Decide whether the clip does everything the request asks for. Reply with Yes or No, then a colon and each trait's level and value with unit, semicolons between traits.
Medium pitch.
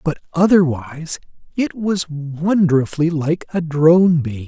Yes: medium, 160 Hz